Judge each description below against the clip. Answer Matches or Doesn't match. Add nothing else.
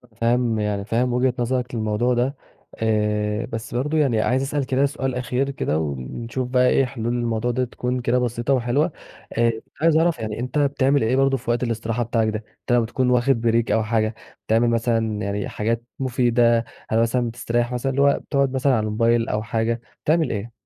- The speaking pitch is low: Matches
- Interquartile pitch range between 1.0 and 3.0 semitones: Matches